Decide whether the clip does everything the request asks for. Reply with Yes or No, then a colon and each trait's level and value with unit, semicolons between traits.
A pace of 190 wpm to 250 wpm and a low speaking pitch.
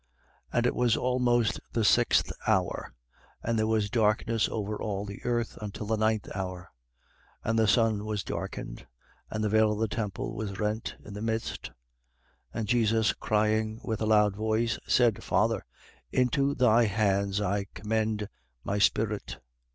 No: average, 160 wpm; low, 110 Hz